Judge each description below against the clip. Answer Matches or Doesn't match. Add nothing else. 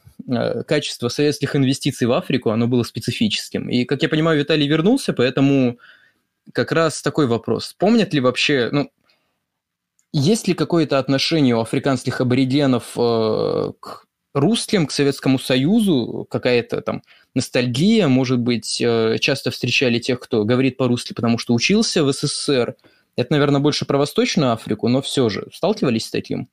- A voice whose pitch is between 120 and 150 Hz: Matches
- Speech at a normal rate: Matches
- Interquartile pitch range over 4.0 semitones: Doesn't match